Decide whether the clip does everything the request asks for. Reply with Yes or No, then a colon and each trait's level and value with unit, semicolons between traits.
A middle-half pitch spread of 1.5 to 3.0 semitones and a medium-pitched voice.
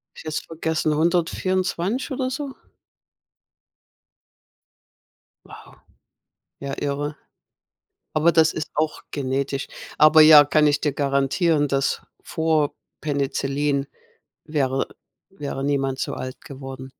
Yes: average, 2.7 semitones; medium, 150 Hz